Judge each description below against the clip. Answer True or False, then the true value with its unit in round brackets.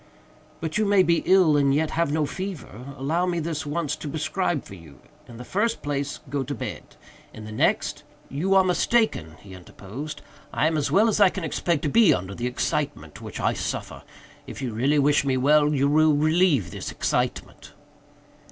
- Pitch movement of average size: True (4.2 semitones)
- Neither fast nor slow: True (195 wpm)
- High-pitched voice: False (150 Hz)